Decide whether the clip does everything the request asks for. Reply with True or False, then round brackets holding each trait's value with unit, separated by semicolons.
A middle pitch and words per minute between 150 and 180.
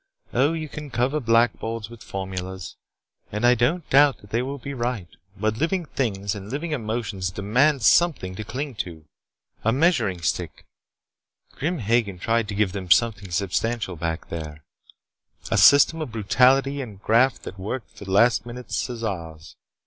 False (115 Hz; 160 wpm)